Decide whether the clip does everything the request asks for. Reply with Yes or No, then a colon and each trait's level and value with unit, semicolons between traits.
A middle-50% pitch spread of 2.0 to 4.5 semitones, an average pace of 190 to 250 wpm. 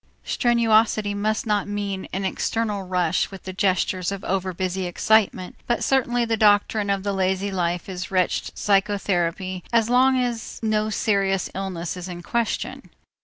No: narrow, 2.6 semitones; average, 150 wpm